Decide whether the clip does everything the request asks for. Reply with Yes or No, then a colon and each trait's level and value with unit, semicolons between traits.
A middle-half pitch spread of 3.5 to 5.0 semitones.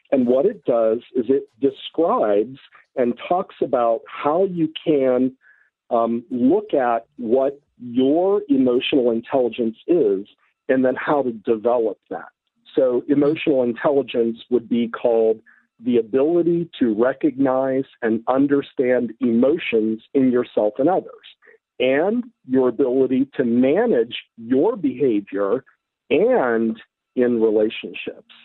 Yes: average, 4.0 semitones